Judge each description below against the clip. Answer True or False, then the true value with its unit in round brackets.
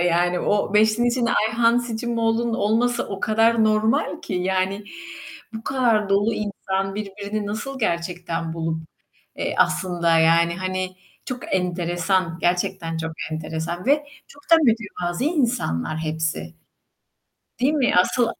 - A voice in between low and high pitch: False (195 Hz)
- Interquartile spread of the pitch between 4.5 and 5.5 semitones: True (4.8 semitones)